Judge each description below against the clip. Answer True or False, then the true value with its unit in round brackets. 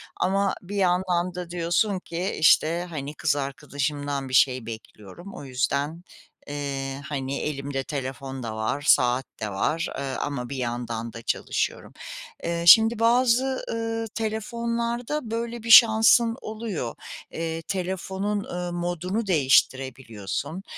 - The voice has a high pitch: False (165 Hz)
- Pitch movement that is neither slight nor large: False (7.1 semitones)